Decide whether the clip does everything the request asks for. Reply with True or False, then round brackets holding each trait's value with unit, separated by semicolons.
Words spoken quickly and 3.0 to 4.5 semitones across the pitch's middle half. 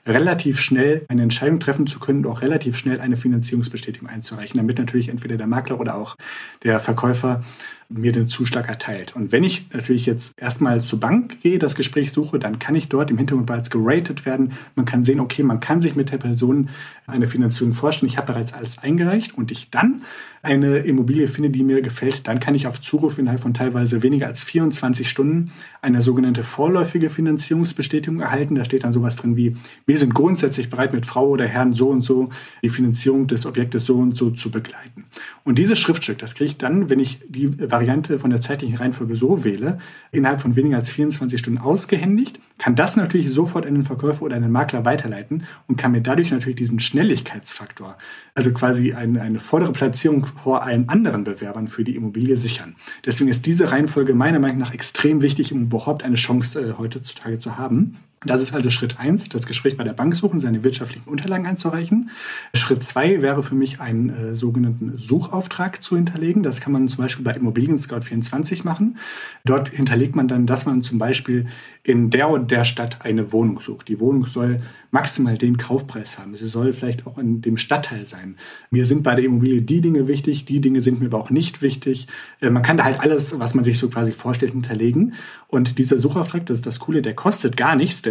True (205 wpm; 3.3 semitones)